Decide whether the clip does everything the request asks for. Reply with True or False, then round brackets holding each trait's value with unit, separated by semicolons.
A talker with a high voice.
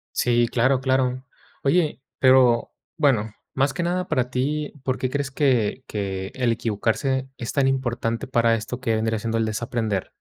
False (125 Hz)